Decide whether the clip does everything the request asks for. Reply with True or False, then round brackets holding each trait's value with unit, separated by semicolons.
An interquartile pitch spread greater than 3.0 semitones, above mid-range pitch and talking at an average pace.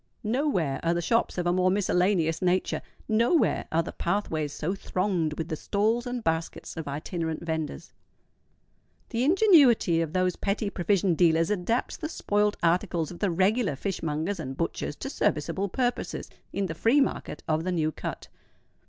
False (4.3 semitones; 180 Hz; 160 wpm)